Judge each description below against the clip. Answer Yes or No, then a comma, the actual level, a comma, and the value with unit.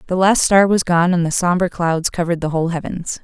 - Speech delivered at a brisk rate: Yes, fast, 240 wpm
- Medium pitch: Yes, medium, 175 Hz